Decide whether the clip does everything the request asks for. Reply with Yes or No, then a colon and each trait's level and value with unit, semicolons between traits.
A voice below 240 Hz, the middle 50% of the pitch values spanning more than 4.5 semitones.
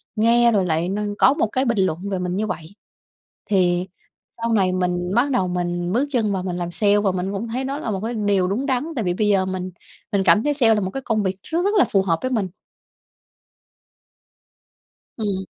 No: high, 200 Hz; average, 4.1 semitones